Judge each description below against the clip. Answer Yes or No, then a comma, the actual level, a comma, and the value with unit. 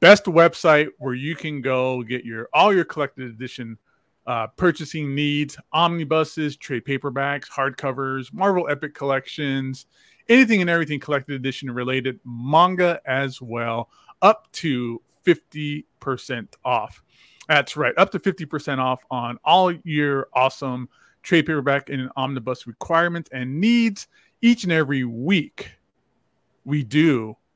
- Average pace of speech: No, slow, 130 wpm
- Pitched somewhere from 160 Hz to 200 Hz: No, medium, 140 Hz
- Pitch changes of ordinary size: Yes, average, 4.1 semitones